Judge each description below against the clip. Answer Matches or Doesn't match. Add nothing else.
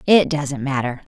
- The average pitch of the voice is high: Doesn't match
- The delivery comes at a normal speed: Matches